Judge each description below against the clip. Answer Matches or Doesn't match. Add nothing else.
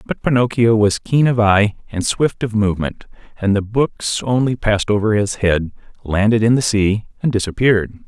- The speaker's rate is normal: Matches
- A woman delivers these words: Doesn't match